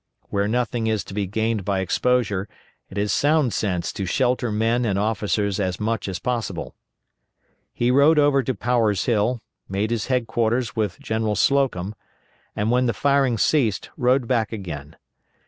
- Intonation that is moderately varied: Yes, average, 3.6 semitones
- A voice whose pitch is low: Yes, low, 110 Hz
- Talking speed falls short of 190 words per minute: Yes, average, 160 wpm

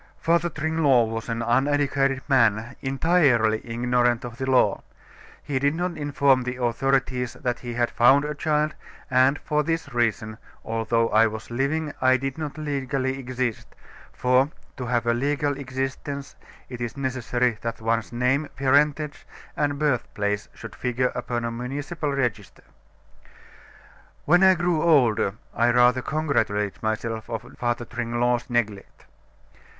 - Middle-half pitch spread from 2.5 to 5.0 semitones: Yes, average, 3.3 semitones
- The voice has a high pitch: No, low, 130 Hz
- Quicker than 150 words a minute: No, average, 140 wpm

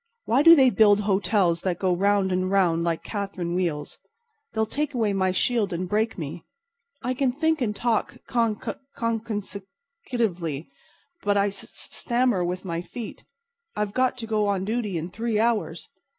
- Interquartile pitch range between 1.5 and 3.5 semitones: No, average, 4.2 semitones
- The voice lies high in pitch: Yes, high, 205 Hz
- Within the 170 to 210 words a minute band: Yes, average, 180 wpm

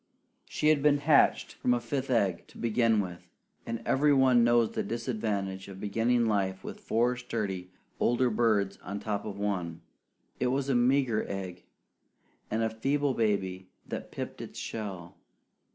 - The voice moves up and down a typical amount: Yes, average, 3.9 semitones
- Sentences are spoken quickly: No, average, 160 wpm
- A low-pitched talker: Yes, low, 115 Hz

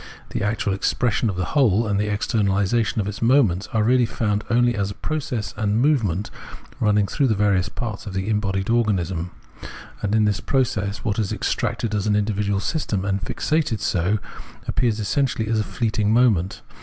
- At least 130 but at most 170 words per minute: No, average, 180 wpm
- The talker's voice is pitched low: Yes, low, 105 Hz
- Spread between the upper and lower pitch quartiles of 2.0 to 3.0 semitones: Yes, average, 2.7 semitones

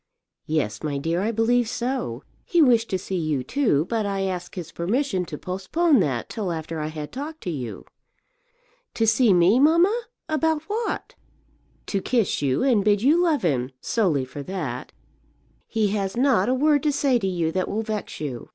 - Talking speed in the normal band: Yes, average, 185 wpm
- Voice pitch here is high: Yes, high, 200 Hz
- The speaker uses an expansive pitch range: Yes, wide, 8.1 semitones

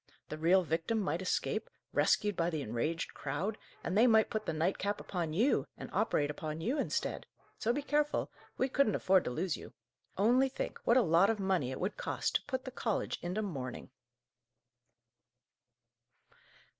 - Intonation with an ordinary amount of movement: No, wide, 5.7 semitones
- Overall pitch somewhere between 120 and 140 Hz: No, high, 190 Hz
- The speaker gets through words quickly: No, average, 170 wpm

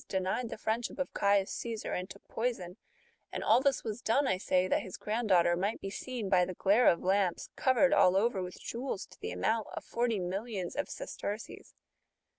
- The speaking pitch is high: Yes, high, 205 Hz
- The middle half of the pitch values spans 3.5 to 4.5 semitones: Yes, average, 4.2 semitones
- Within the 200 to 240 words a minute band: Yes, fast, 205 wpm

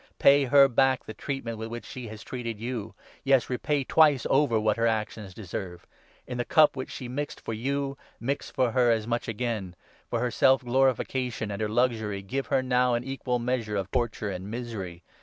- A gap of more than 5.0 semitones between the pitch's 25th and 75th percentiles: No, average, 3.2 semitones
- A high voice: No, low, 120 Hz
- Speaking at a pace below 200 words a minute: No, fast, 205 wpm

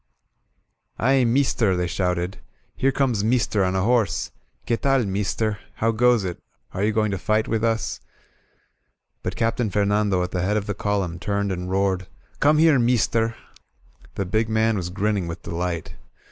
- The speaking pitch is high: No, low, 105 Hz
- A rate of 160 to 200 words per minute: Yes, average, 170 wpm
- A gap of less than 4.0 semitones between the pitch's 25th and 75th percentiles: Yes, average, 3.4 semitones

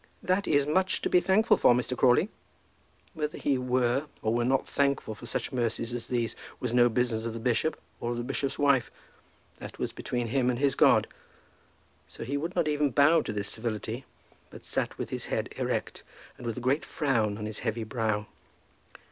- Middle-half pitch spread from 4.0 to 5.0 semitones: No, average, 3.5 semitones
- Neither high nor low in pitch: No, low, 125 Hz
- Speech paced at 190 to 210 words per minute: Yes, average, 200 wpm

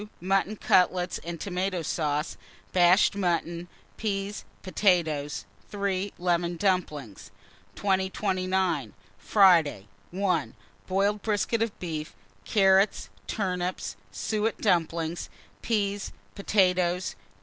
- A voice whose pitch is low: No, medium, 185 Hz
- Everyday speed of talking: No, slow, 85 wpm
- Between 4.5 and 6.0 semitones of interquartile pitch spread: No, narrow, 2.6 semitones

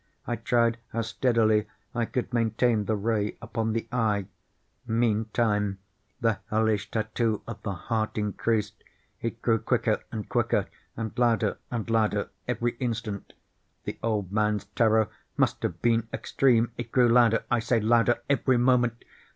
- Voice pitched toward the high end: No, low, 115 Hz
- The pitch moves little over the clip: Yes, narrow, 1.7 semitones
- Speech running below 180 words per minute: Yes, average, 145 wpm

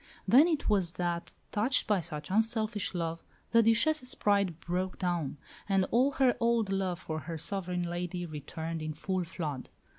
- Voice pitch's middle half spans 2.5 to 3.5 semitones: No, average, 4.7 semitones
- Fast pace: No, average, 160 wpm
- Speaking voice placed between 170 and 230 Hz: Yes, medium, 185 Hz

